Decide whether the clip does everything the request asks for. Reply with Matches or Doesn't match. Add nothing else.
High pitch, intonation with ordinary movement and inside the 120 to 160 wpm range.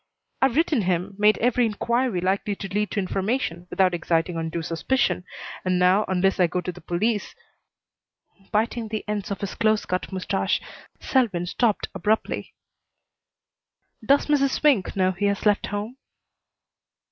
Matches